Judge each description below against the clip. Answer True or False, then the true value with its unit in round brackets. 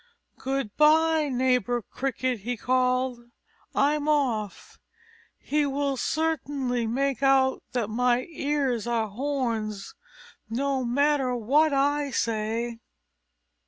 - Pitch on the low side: False (260 Hz)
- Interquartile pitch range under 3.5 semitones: True (3.1 semitones)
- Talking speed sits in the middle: False (95 wpm)